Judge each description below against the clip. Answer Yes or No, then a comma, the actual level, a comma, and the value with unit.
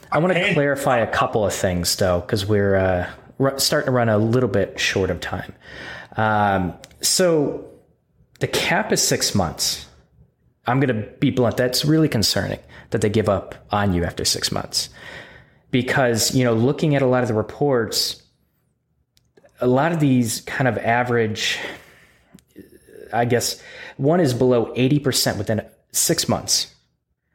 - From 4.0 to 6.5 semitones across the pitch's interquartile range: Yes, average, 4.5 semitones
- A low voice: Yes, low, 120 Hz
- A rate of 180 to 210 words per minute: No, average, 160 wpm